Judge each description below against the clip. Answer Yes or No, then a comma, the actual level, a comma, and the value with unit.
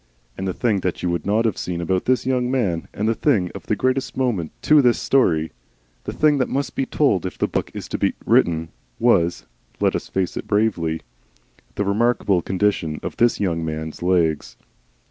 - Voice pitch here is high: No, low, 100 Hz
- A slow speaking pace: No, average, 200 wpm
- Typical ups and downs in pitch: No, wide, 6.2 semitones